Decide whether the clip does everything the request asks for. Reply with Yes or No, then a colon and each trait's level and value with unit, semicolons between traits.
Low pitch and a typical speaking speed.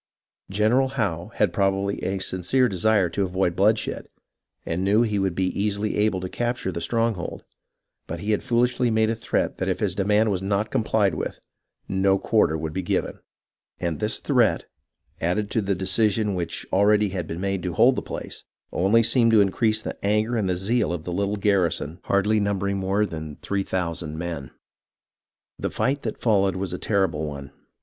Yes: low, 100 Hz; average, 180 wpm